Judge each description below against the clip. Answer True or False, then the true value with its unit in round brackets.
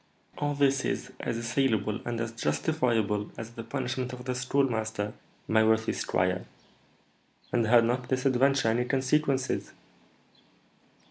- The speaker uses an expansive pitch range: False (2.9 semitones)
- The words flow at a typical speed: False (130 wpm)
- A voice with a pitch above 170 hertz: False (120 Hz)